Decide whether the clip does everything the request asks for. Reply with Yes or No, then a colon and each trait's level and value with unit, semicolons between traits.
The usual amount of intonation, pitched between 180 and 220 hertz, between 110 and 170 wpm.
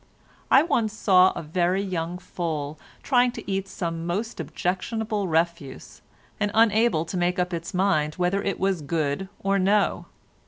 Yes: average, 3.2 semitones; medium, 185 Hz; average, 155 wpm